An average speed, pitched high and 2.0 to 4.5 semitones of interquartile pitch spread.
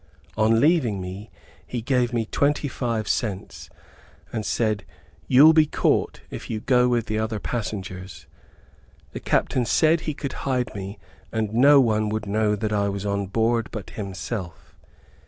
No: average, 155 wpm; low, 110 Hz; average, 3.5 semitones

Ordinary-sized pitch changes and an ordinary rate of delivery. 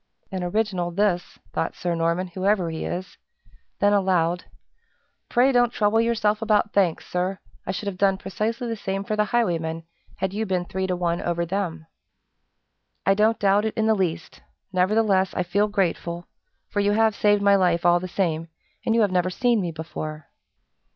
Yes: average, 3.2 semitones; average, 180 wpm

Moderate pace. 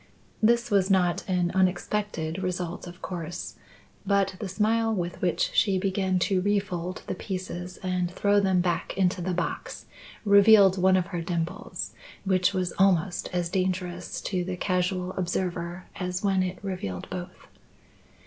Yes: average, 150 wpm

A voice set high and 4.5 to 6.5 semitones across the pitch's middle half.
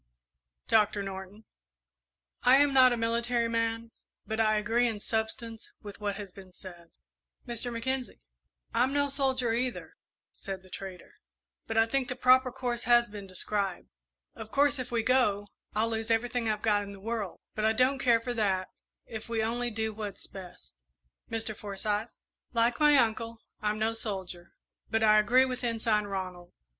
No: high, 225 Hz; average, 2.7 semitones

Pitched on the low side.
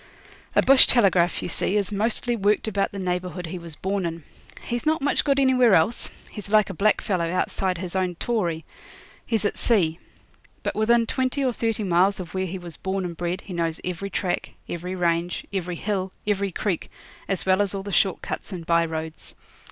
No: high, 190 Hz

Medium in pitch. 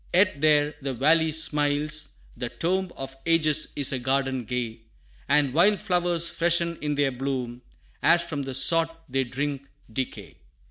Yes: medium, 145 Hz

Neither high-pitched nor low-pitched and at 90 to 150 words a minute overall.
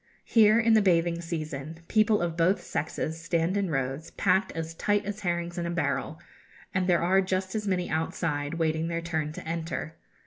No: medium, 170 Hz; average, 185 wpm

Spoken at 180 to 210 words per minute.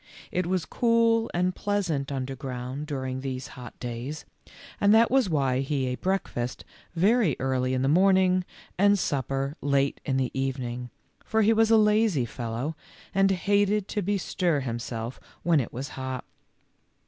No: average, 155 wpm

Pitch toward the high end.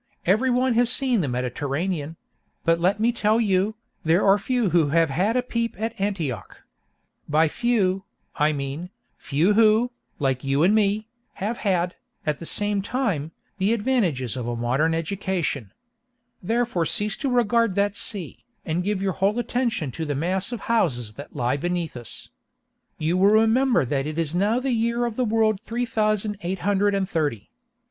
Yes: high, 195 Hz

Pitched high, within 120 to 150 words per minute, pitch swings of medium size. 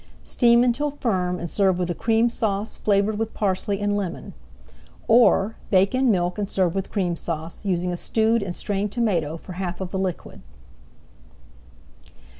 No: high, 195 Hz; average, 160 wpm; average, 3.6 semitones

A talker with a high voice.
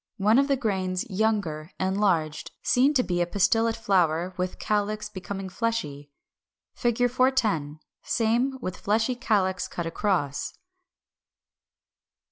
Yes: high, 205 Hz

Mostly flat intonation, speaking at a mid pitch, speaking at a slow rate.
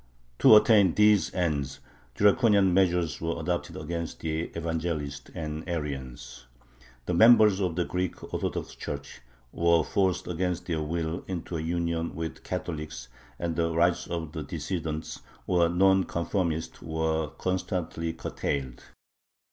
No: narrow, 2.2 semitones; very low, 85 Hz; slow, 130 wpm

